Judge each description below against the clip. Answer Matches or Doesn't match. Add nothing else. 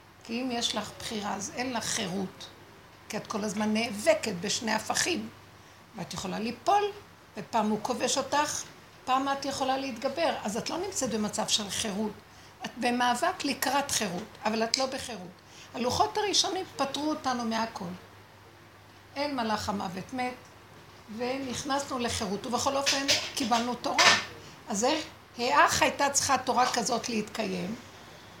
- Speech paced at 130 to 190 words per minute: Matches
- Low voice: Doesn't match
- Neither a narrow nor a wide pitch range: Matches